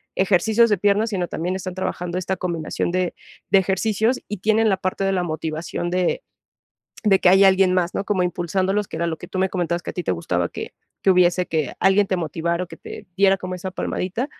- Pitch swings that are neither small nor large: No, narrow, 2.0 semitones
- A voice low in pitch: No, medium, 185 Hz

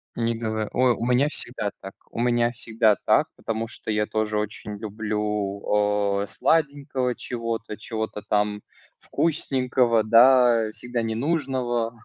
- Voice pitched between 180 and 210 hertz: No, low, 115 Hz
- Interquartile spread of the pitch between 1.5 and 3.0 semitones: Yes, narrow, 2.6 semitones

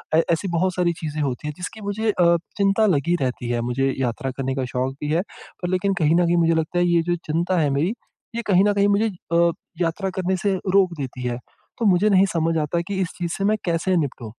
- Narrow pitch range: No, average, 4.6 semitones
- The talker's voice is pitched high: No, medium, 170 Hz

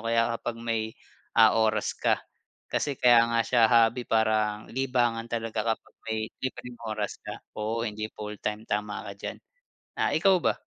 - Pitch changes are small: Yes, narrow, 1.6 semitones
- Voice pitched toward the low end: Yes, low, 115 Hz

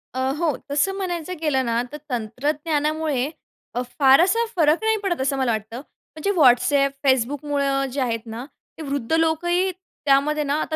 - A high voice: Yes, very high, 290 Hz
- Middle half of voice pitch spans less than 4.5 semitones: Yes, average, 3.6 semitones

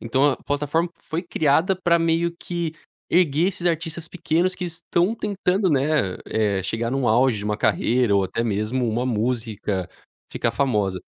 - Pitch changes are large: Yes, wide, 7.2 semitones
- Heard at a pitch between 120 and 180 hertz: Yes, medium, 140 Hz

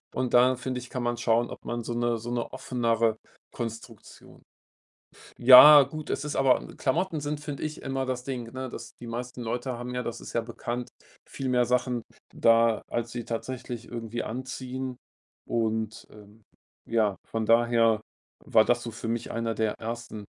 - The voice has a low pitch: Yes, low, 120 Hz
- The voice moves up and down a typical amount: No, narrow, 1.9 semitones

